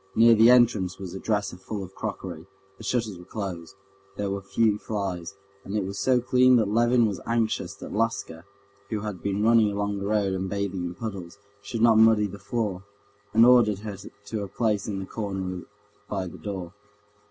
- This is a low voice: Yes, low, 100 Hz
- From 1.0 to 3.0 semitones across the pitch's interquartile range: Yes, average, 2.7 semitones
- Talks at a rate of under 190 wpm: No, average, 195 wpm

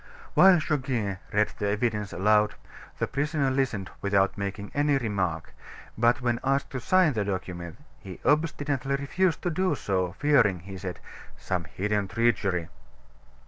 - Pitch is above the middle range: No, low, 110 Hz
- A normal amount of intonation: No, wide, 6.2 semitones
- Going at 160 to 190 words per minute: No, average, 140 wpm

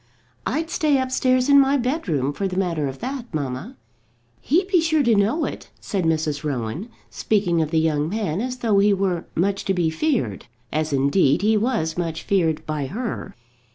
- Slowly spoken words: No, average, 185 wpm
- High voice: Yes, high, 195 Hz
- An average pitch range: No, wide, 8.2 semitones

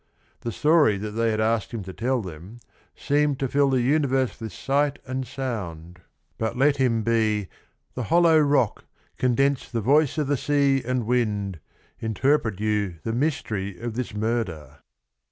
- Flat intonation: No, average, 4.3 semitones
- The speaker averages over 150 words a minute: Yes, average, 160 wpm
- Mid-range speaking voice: No, low, 120 Hz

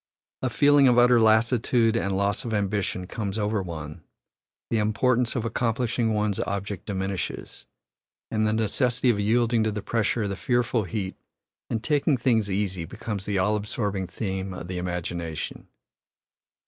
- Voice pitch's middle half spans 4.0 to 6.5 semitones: No, average, 3.3 semitones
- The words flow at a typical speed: Yes, average, 155 wpm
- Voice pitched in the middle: No, low, 105 Hz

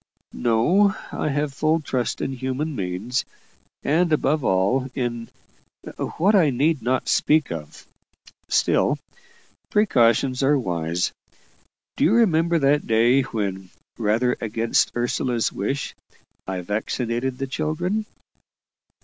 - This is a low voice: Yes, low, 130 Hz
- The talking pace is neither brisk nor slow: No, slow, 115 wpm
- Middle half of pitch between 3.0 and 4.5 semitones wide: No, average, 5.1 semitones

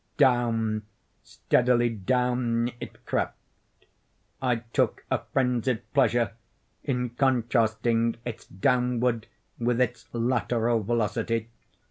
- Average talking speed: No, slow, 85 wpm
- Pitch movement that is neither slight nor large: No, narrow, 1.5 semitones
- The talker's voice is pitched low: Yes, low, 120 Hz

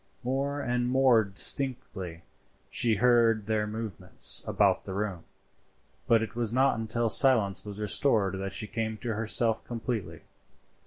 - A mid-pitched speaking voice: No, low, 115 Hz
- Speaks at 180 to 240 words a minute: No, average, 140 wpm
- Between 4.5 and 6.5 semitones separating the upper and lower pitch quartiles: No, narrow, 2.6 semitones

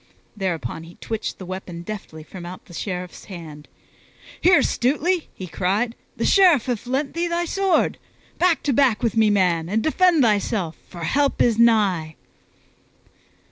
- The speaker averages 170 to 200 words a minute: No, average, 155 wpm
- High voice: Yes, high, 215 Hz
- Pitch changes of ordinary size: No, wide, 7.8 semitones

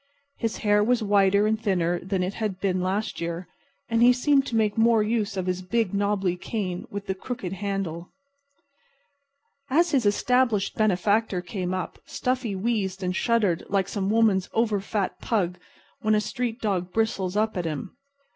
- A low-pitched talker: No, high, 205 Hz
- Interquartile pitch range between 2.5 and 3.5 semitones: Yes, average, 3.2 semitones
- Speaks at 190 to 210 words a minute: No, average, 170 wpm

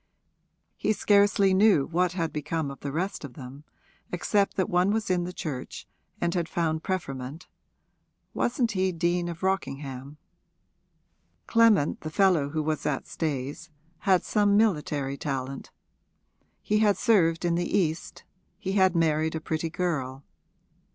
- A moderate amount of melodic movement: Yes, average, 4.2 semitones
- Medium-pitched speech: Yes, medium, 170 Hz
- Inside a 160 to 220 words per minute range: No, average, 145 wpm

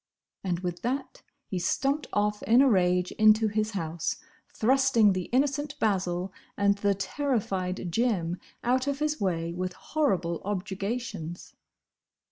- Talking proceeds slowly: Yes, slow, 130 wpm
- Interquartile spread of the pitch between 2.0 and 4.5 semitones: No, wide, 5.6 semitones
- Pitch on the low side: No, high, 205 Hz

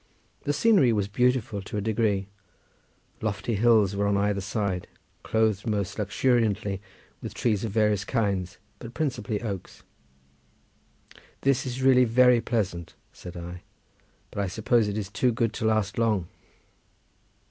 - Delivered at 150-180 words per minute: No, average, 140 wpm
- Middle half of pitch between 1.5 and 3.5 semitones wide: Yes, average, 3.0 semitones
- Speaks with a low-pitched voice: Yes, low, 105 Hz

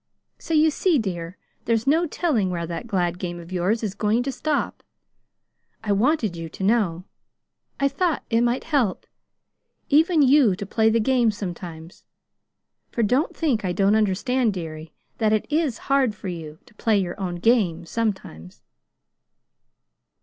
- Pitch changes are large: Yes, wide, 6.4 semitones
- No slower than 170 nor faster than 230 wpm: No, average, 155 wpm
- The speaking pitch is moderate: No, high, 215 Hz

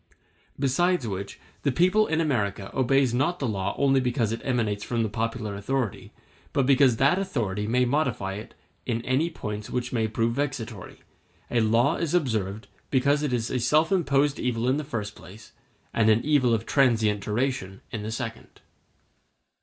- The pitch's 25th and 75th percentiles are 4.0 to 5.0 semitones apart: Yes, average, 4.3 semitones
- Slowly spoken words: No, average, 170 wpm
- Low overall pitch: Yes, low, 120 Hz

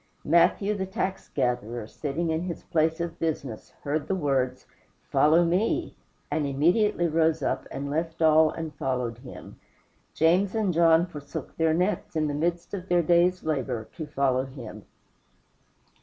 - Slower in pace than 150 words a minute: No, average, 155 wpm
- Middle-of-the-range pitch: Yes, medium, 160 Hz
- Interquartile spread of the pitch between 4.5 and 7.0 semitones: No, average, 3.8 semitones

